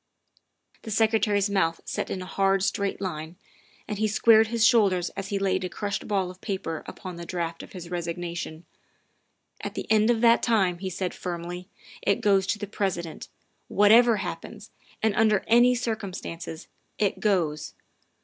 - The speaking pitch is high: Yes, high, 195 Hz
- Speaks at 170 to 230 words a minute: Yes, average, 180 wpm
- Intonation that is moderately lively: Yes, average, 3.4 semitones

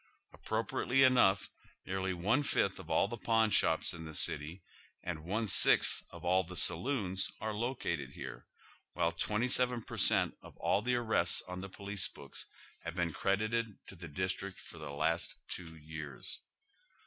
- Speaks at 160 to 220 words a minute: Yes, average, 170 wpm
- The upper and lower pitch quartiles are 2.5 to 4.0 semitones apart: No, average, 4.7 semitones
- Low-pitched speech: Yes, very low, 95 Hz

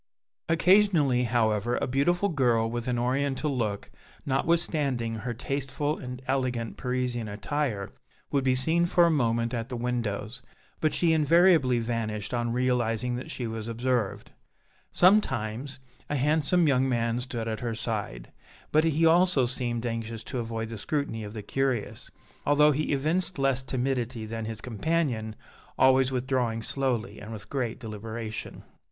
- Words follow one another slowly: No, average, 145 wpm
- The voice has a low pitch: Yes, low, 125 Hz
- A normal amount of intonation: Yes, average, 3.7 semitones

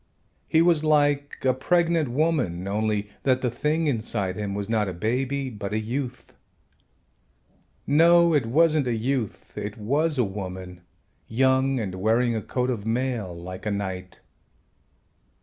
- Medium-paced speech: Yes, average, 150 wpm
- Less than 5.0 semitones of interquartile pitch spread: No, wide, 5.6 semitones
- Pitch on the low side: Yes, low, 120 Hz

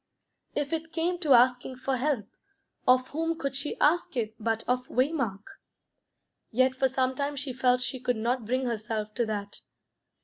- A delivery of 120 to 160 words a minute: No, average, 170 wpm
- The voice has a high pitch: Yes, very high, 255 Hz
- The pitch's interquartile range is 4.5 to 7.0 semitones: No, average, 3.0 semitones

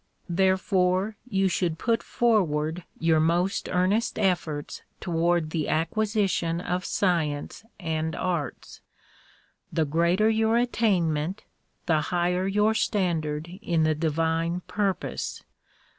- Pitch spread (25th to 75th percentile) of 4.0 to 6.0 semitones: No, average, 3.3 semitones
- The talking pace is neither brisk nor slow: No, slow, 110 wpm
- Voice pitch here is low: No, medium, 175 Hz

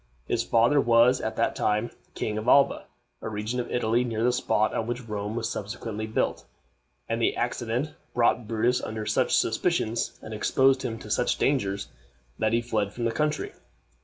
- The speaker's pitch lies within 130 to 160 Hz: No, low, 115 Hz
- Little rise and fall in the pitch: Yes, narrow, 2.2 semitones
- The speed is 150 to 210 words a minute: Yes, average, 180 wpm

